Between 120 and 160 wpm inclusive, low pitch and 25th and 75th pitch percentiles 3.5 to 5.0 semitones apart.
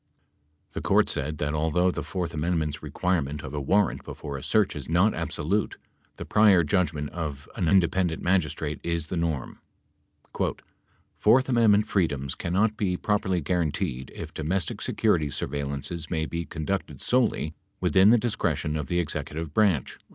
Yes: average, 150 wpm; very low, 85 Hz; average, 4.4 semitones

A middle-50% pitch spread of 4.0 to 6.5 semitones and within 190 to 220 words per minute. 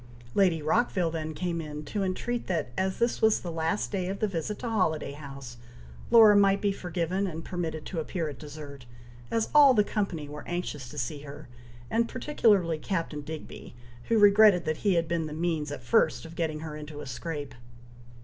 Yes: average, 4.7 semitones; average, 195 wpm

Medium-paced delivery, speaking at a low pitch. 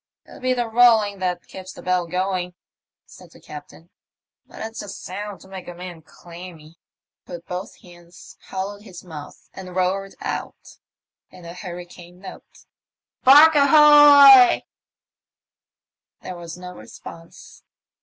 No: average, 155 wpm; medium, 185 Hz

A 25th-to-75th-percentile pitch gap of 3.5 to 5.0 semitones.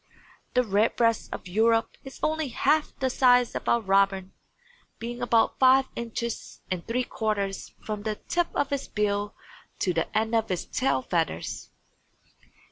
Yes: average, 3.8 semitones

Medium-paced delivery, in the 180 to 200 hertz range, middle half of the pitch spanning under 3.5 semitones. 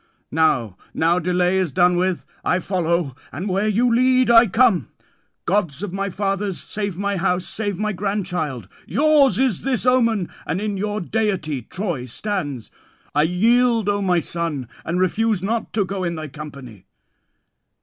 No: average, 160 wpm; high, 190 Hz; average, 4.0 semitones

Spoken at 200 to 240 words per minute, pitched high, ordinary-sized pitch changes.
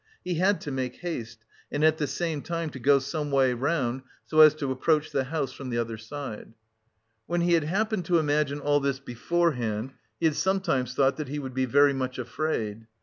No: fast, 205 wpm; medium, 145 Hz; average, 3.6 semitones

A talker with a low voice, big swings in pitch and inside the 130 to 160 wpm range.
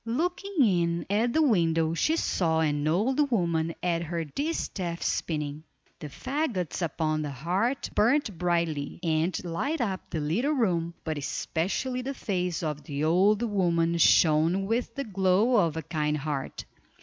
No: medium, 175 Hz; wide, 6.1 semitones; average, 150 wpm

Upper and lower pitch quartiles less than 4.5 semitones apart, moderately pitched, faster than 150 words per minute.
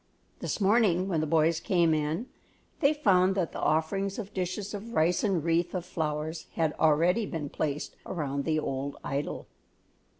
Yes: average, 3.8 semitones; medium, 170 Hz; average, 165 wpm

